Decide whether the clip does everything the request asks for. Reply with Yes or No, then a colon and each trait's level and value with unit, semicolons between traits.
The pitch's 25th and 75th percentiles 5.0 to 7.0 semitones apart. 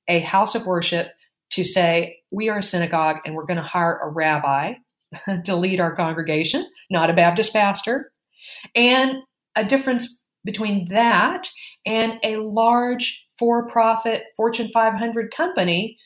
Yes: average, 5.3 semitones